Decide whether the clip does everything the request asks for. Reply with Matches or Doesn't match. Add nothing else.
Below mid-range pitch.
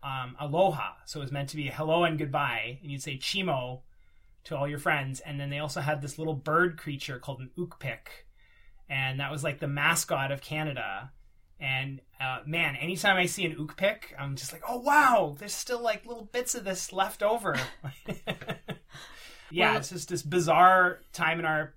Doesn't match